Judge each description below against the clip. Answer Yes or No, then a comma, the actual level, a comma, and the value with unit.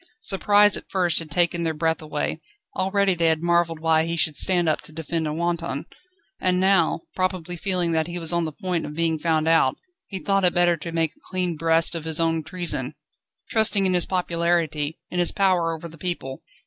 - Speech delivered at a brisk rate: Yes, fast, 210 wpm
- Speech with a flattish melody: Yes, narrow, 2.0 semitones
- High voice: No, medium, 170 Hz